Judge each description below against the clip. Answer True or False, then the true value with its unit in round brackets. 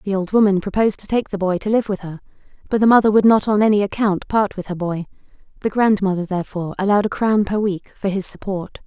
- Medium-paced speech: False (235 wpm)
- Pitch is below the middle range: False (200 Hz)